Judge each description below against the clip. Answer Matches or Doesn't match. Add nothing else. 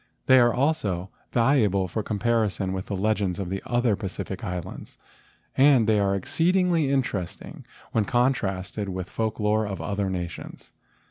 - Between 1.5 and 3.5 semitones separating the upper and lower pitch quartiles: Doesn't match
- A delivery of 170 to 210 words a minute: Doesn't match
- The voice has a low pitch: Matches